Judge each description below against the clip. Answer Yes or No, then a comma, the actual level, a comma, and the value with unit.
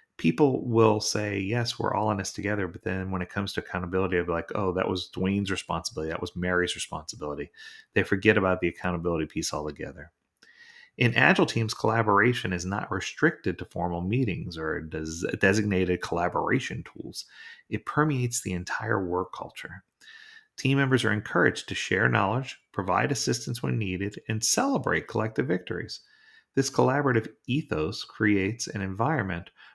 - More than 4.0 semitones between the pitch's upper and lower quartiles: Yes, average, 5.1 semitones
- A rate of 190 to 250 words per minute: No, average, 155 wpm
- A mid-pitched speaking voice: No, low, 100 Hz